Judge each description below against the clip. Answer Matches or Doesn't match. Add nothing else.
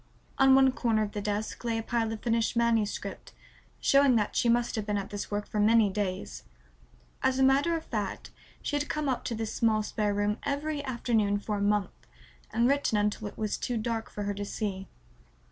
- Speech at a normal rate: Doesn't match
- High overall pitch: Matches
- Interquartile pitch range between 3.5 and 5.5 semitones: Doesn't match